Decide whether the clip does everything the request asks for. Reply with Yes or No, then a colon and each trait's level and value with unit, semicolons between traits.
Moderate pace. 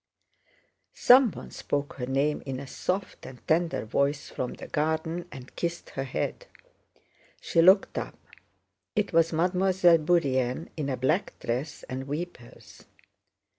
No: slow, 130 wpm